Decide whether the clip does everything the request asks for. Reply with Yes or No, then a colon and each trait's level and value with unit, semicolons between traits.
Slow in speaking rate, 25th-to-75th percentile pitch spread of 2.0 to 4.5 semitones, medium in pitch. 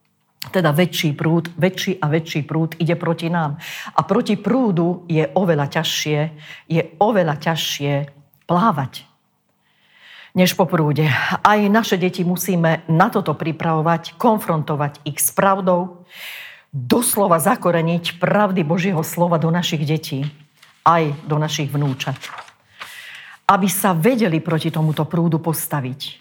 No: average, 120 wpm; average, 2.8 semitones; medium, 165 Hz